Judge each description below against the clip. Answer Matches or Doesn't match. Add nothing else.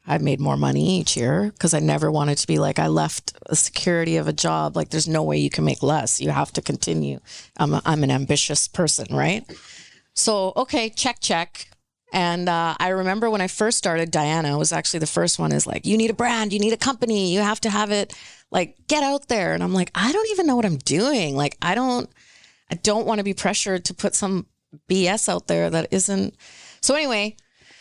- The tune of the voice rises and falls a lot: Matches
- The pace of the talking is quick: Matches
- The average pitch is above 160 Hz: Matches